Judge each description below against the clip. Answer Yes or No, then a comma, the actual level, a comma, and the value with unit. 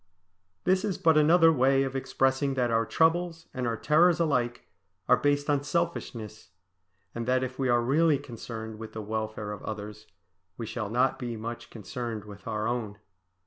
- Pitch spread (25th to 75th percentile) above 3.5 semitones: Yes, average, 4.6 semitones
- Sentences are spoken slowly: No, average, 175 wpm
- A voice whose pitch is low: Yes, low, 125 Hz